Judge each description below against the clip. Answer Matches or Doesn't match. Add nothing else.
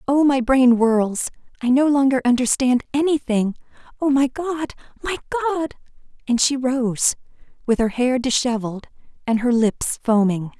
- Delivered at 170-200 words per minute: Doesn't match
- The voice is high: Matches